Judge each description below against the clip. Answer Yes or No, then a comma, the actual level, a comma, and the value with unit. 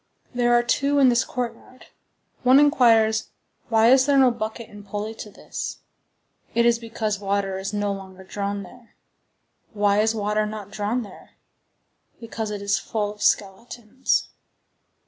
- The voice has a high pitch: Yes, high, 220 Hz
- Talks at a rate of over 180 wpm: No, average, 150 wpm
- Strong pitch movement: No, average, 2.8 semitones